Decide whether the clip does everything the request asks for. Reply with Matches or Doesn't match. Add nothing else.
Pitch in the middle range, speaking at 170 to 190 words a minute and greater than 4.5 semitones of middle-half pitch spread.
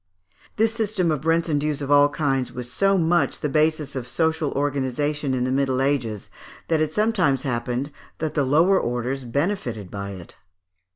Doesn't match